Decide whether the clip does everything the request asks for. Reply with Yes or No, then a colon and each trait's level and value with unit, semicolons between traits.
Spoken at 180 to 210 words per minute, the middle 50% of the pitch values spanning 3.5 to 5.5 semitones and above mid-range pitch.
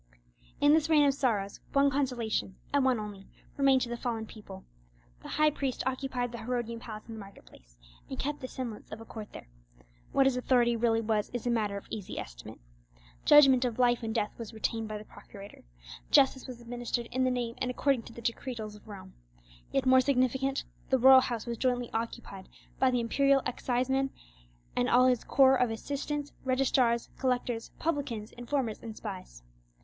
No: average, 185 wpm; average, 2.9 semitones; high, 245 Hz